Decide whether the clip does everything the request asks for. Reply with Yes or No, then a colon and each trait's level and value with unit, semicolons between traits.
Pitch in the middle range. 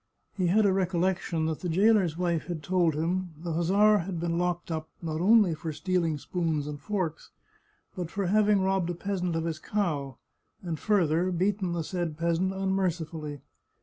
Yes: medium, 175 Hz